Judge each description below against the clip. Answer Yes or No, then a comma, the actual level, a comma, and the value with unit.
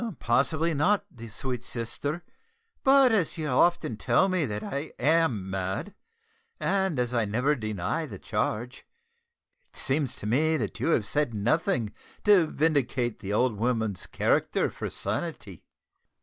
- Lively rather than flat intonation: Yes, wide, 6.7 semitones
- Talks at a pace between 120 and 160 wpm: Yes, average, 140 wpm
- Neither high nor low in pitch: No, low, 130 Hz